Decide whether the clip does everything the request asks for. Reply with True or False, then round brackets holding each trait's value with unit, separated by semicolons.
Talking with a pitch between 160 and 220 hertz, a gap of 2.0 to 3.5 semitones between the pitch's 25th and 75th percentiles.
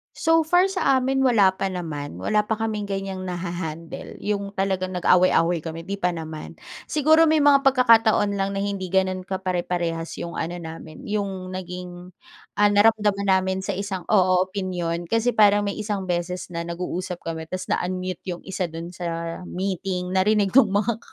True (190 Hz; 2.8 semitones)